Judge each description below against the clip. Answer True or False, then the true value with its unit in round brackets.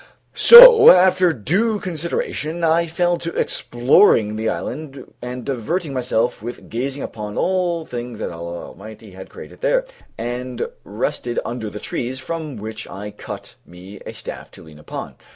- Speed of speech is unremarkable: True (160 wpm)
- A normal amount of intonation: False (7.6 semitones)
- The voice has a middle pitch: False (125 Hz)